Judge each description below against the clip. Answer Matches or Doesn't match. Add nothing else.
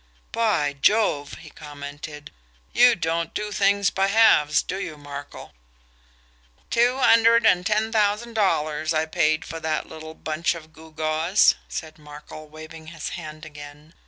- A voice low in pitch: Doesn't match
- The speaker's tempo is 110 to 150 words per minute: Matches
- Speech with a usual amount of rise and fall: Matches